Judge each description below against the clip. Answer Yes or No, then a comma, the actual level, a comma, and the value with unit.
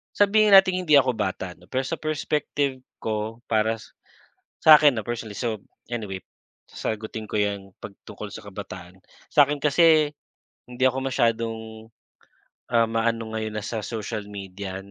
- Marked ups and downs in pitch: No, average, 5.0 semitones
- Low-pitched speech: Yes, low, 115 Hz